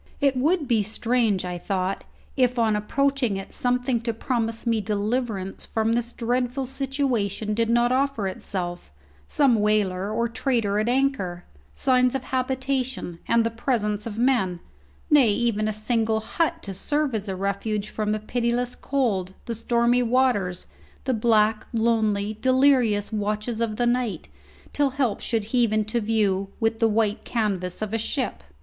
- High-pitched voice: Yes, high, 225 Hz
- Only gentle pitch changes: No, average, 3.1 semitones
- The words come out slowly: No, average, 160 wpm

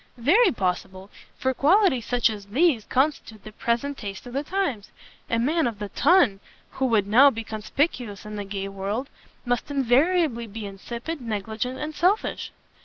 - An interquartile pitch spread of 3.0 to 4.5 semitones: No, wide, 5.4 semitones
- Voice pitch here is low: No, high, 235 Hz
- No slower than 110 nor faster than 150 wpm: No, average, 165 wpm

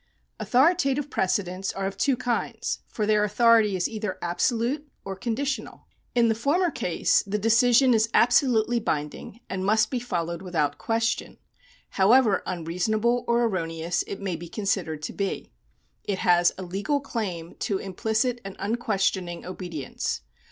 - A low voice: No, high, 210 Hz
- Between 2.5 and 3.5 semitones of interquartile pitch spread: No, average, 4.5 semitones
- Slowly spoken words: No, average, 145 wpm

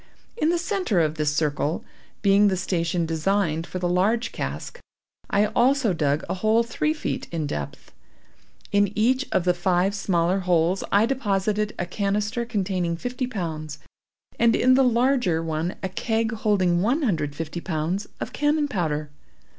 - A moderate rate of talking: Yes, average, 160 wpm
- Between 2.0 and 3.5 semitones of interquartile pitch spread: No, average, 5.3 semitones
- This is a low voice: No, high, 195 Hz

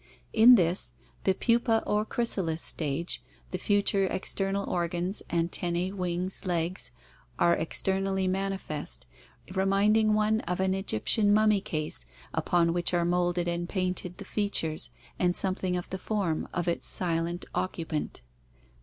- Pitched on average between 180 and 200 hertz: Yes, medium, 185 Hz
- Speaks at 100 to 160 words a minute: Yes, average, 140 wpm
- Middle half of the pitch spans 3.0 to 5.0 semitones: No, narrow, 2.4 semitones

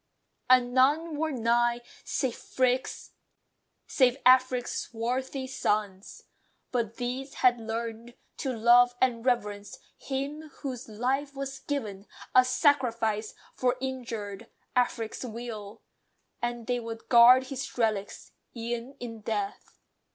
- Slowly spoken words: Yes, slow, 105 wpm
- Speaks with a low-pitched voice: No, high, 245 Hz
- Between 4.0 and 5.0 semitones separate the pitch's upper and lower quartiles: No, narrow, 2.4 semitones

